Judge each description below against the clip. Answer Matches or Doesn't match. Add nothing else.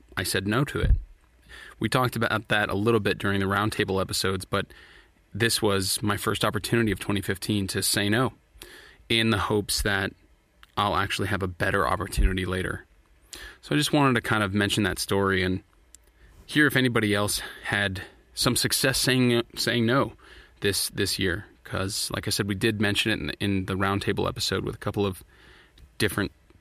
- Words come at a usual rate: Matches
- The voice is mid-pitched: Doesn't match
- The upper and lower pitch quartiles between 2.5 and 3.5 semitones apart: Matches